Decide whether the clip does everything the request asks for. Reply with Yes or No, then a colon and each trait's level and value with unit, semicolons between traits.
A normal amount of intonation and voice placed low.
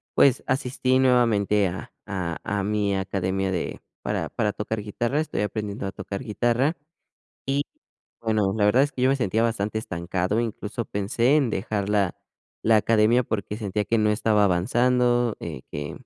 Yes: average, 3.4 semitones; low, 105 Hz